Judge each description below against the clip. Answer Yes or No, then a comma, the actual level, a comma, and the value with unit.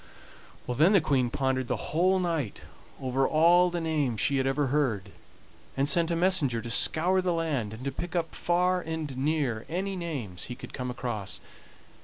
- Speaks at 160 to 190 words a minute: Yes, average, 180 wpm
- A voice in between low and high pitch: Yes, medium, 150 Hz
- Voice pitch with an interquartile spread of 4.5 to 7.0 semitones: Yes, average, 5.2 semitones